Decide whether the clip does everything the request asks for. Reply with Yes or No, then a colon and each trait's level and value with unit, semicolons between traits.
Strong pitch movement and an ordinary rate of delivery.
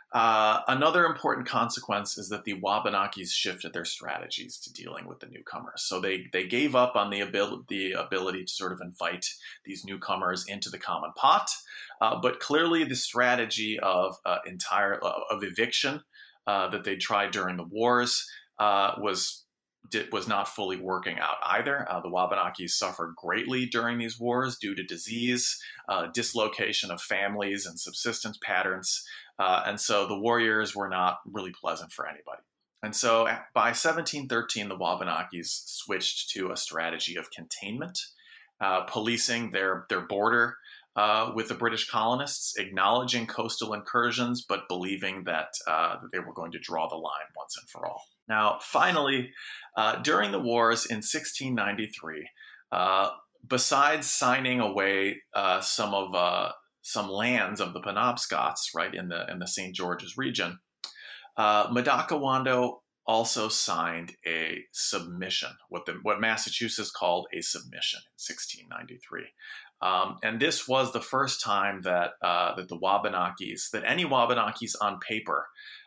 No: average, 4.3 semitones; average, 155 wpm